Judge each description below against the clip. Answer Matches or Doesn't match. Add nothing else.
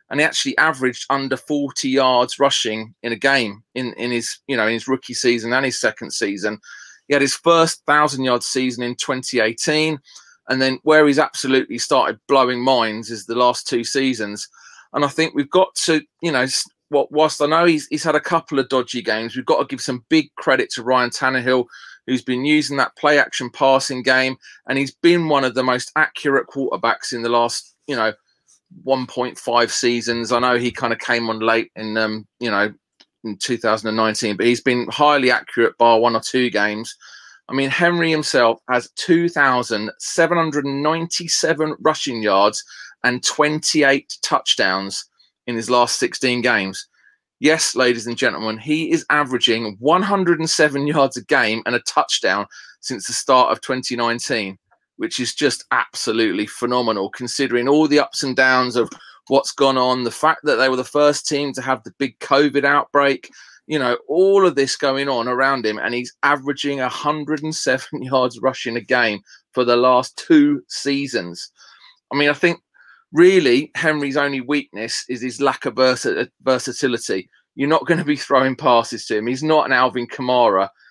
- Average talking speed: Matches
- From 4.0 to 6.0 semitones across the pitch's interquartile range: Doesn't match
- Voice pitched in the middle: Doesn't match